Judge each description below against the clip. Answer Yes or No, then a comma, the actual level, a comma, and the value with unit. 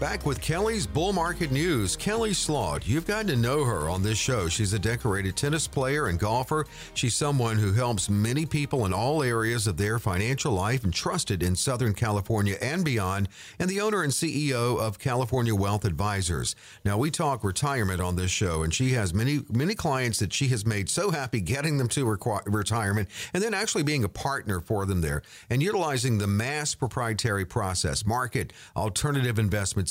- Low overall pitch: Yes, low, 120 Hz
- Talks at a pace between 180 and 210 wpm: Yes, average, 190 wpm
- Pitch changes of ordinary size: No, wide, 5.7 semitones